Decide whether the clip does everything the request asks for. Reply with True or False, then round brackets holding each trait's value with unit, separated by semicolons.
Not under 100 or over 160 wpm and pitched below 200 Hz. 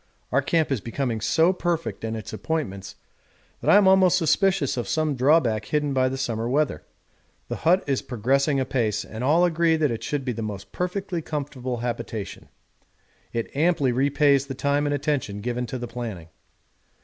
False (175 wpm; 135 Hz)